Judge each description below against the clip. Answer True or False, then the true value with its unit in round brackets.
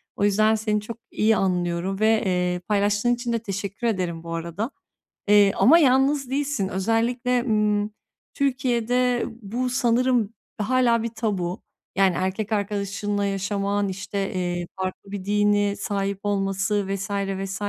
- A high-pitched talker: True (205 Hz)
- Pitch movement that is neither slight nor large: True (3.0 semitones)